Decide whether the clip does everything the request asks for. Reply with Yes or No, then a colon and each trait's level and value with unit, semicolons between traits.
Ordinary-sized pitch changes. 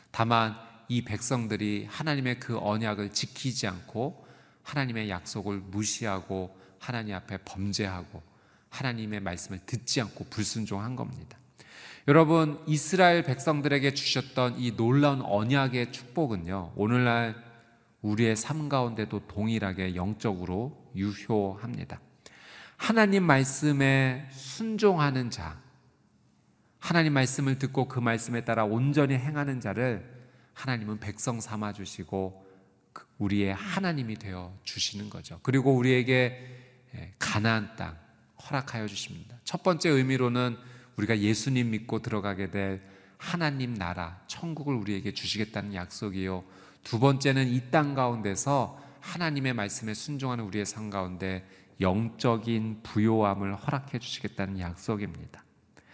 Yes: average, 4.7 semitones